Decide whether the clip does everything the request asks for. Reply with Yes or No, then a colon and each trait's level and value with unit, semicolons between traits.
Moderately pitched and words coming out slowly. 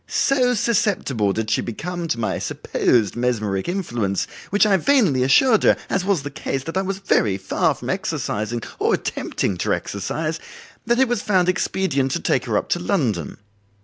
No: medium, 155 Hz; average, 180 wpm